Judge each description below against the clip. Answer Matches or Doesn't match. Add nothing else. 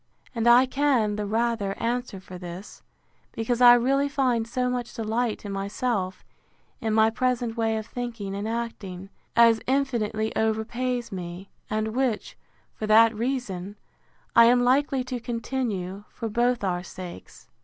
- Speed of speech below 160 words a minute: Matches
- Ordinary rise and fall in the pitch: Matches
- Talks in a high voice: Matches